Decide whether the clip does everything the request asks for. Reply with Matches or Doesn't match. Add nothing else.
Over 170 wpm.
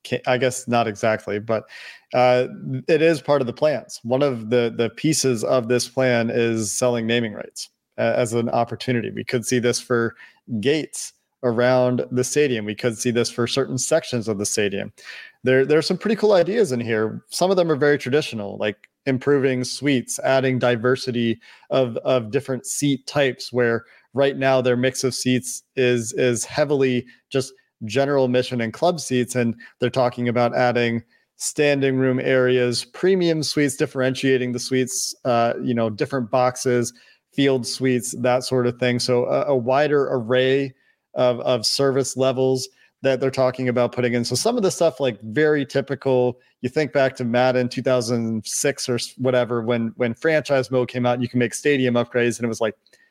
Matches